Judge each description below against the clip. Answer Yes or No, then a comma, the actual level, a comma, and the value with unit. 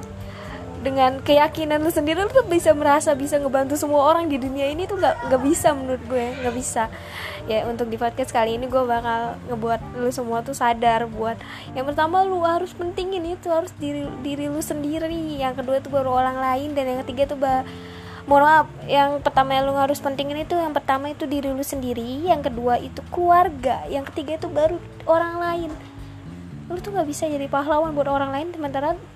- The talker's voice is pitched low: No, very high, 280 Hz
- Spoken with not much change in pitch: No, average, 3.5 semitones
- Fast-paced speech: Yes, fast, 190 wpm